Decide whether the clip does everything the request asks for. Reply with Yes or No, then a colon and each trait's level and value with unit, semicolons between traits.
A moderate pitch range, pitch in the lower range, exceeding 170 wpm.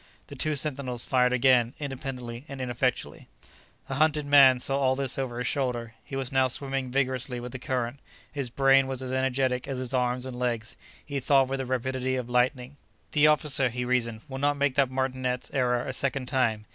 No: narrow, 1.5 semitones; low, 130 Hz; average, 195 wpm